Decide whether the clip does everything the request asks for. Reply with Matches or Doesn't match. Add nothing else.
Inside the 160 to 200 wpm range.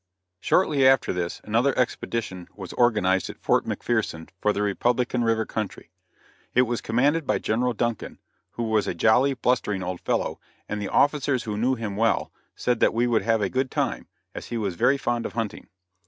Matches